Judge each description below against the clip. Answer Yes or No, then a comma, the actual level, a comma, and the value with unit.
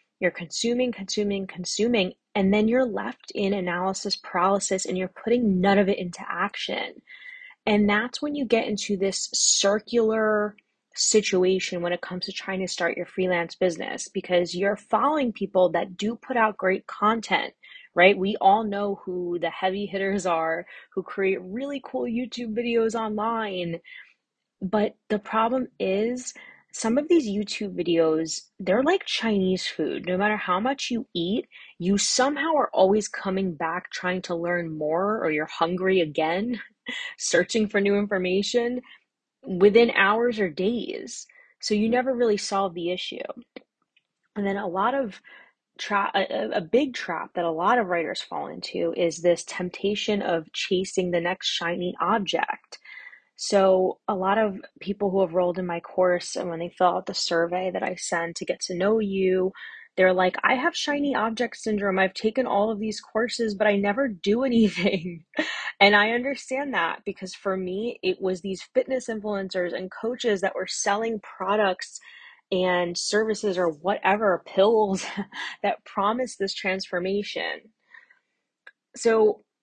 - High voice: Yes, high, 200 Hz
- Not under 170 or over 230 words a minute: No, average, 160 wpm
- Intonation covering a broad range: No, average, 3.8 semitones